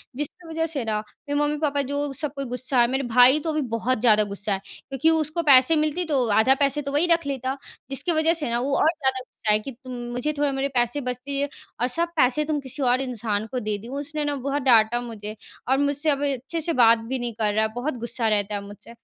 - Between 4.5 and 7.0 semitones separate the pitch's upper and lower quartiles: No, average, 3.6 semitones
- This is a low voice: No, very high, 265 Hz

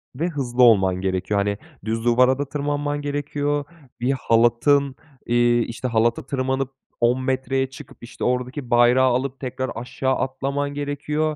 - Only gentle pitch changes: No, average, 3.0 semitones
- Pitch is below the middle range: Yes, low, 130 Hz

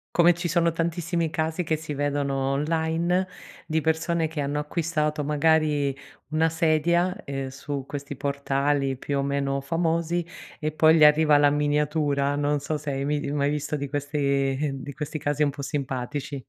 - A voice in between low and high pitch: Yes, medium, 150 Hz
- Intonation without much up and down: Yes, narrow, 2.2 semitones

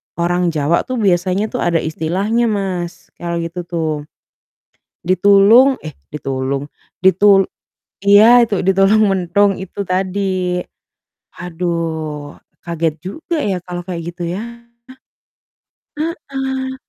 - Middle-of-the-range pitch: Yes, medium, 180 Hz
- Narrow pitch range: No, average, 3.3 semitones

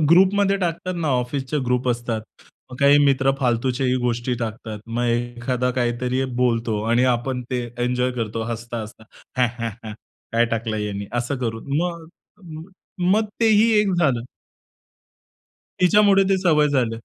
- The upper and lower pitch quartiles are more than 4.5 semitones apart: Yes, average, 5.1 semitones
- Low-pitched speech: Yes, low, 125 Hz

